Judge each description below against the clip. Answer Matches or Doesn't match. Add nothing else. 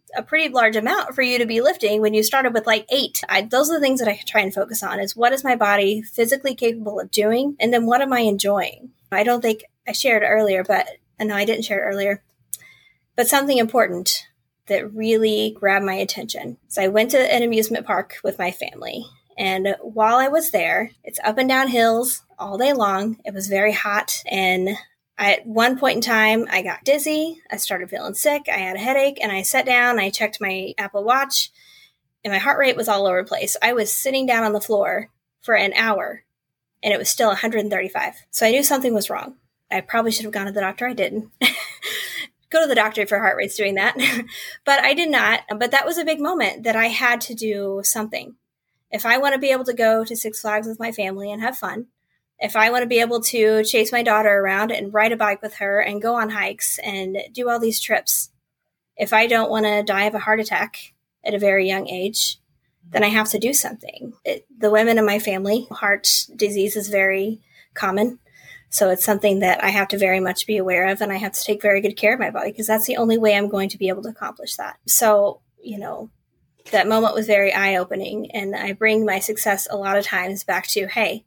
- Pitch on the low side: Doesn't match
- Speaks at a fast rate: Matches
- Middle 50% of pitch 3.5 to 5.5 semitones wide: Doesn't match